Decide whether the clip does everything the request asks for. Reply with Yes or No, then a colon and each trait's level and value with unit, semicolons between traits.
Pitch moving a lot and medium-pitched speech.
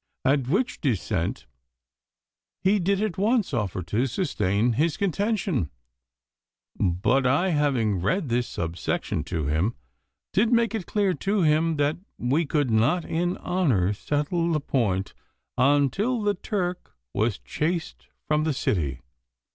Yes: wide, 8.8 semitones; medium, 145 Hz